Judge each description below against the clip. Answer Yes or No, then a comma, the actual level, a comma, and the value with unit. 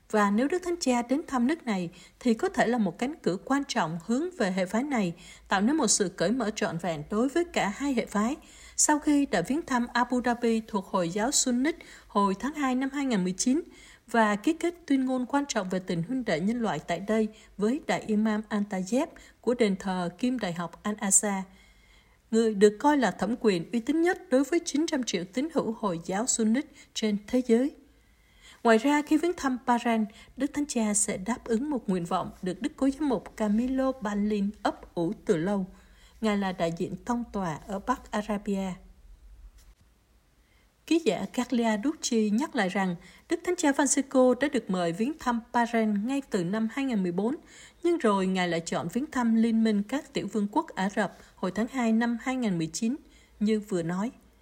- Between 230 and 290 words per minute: No, average, 200 wpm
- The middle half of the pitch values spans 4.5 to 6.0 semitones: Yes, average, 4.8 semitones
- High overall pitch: Yes, high, 225 Hz